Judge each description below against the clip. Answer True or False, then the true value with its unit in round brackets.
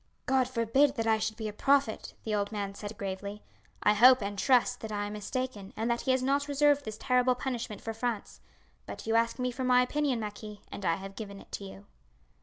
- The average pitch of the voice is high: True (225 Hz)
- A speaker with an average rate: False (225 wpm)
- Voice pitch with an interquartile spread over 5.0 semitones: False (3.7 semitones)